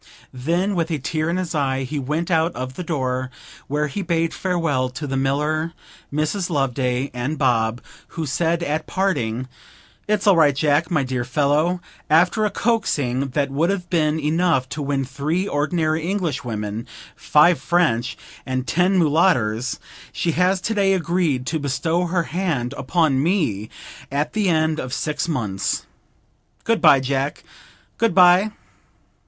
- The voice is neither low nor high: Yes, medium, 155 Hz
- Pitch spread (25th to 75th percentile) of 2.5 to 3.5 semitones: No, average, 4.7 semitones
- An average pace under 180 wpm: Yes, average, 155 wpm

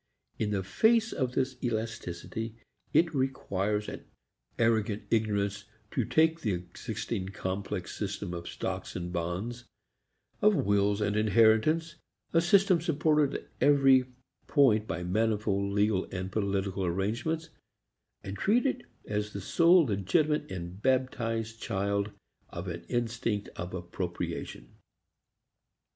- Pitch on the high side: No, low, 110 Hz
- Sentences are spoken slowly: Yes, slow, 120 wpm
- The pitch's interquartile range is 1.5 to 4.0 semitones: No, average, 5.3 semitones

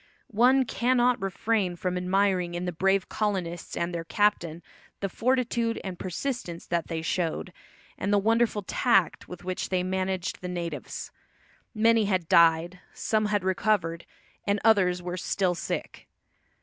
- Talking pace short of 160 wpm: Yes, average, 145 wpm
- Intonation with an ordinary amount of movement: Yes, average, 3.4 semitones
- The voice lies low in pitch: No, medium, 185 Hz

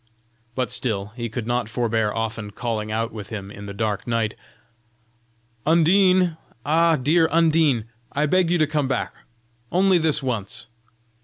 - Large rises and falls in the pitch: Yes, wide, 6.7 semitones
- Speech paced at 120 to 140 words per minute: No, average, 150 wpm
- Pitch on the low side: Yes, low, 125 Hz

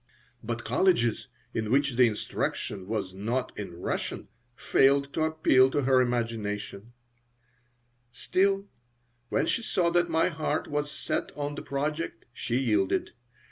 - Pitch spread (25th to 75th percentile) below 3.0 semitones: No, average, 5.0 semitones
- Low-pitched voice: Yes, low, 130 Hz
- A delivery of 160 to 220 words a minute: No, slow, 135 wpm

